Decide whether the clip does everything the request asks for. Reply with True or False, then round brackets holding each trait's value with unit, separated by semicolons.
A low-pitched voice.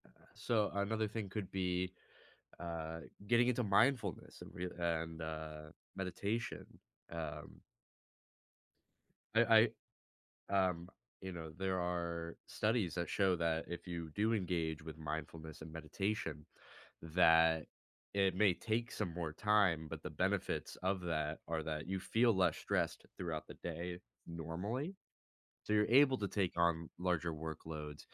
True (90 Hz)